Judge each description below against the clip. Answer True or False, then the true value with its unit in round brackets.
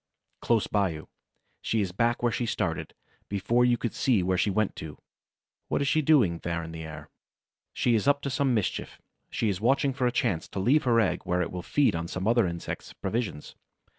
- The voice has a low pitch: True (105 Hz)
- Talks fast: True (215 wpm)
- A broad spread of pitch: True (5.7 semitones)